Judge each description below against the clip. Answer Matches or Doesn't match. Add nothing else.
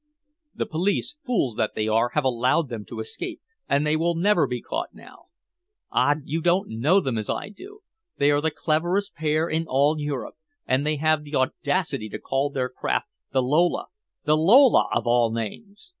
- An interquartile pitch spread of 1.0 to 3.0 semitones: Doesn't match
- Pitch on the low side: Doesn't match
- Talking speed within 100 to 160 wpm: Doesn't match